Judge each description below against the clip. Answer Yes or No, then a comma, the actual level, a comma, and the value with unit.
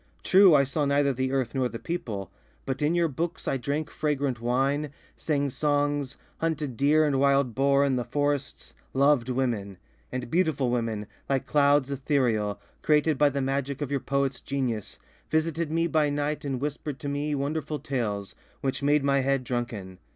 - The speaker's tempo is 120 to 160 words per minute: No, average, 175 wpm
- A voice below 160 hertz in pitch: Yes, medium, 140 Hz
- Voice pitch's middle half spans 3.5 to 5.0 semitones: No, narrow, 2.5 semitones